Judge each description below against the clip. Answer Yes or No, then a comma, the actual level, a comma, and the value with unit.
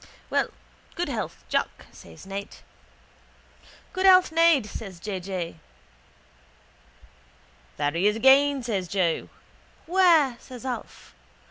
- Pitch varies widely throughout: Yes, wide, 7.6 semitones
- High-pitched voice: Yes, high, 225 Hz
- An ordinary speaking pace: No, slow, 115 wpm